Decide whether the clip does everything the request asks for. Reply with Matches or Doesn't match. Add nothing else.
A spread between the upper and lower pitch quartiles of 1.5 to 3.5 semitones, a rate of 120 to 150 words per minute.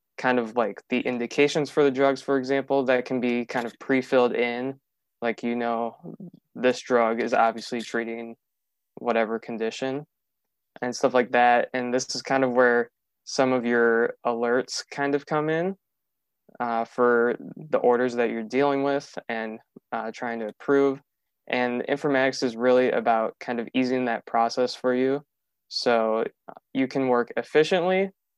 Doesn't match